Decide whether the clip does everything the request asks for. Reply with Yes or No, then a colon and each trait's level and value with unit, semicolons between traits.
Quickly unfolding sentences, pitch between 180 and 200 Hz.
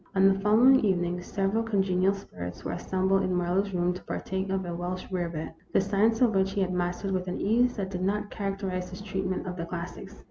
Yes: fast, 215 wpm; high, 190 Hz